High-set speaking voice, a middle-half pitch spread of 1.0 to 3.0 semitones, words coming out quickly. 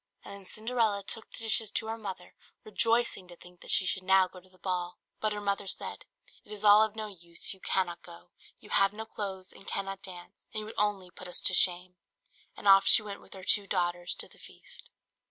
Yes: high, 195 Hz; narrow, 2.6 semitones; fast, 230 wpm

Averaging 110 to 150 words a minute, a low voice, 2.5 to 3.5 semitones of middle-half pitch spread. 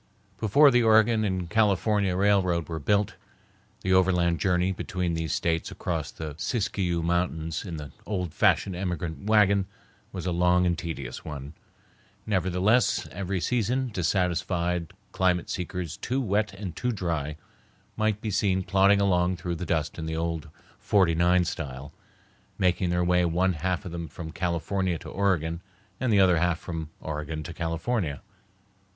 Yes: average, 145 wpm; very low, 90 Hz; average, 3.0 semitones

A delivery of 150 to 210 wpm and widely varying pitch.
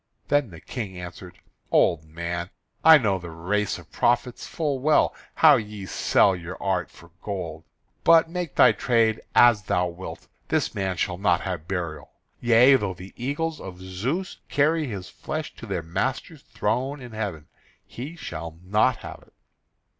Yes: average, 160 wpm; wide, 6.6 semitones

